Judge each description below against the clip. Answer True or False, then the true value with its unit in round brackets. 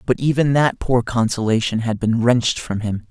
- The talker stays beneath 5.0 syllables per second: False (5.1 syllables/s)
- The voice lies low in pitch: True (120 Hz)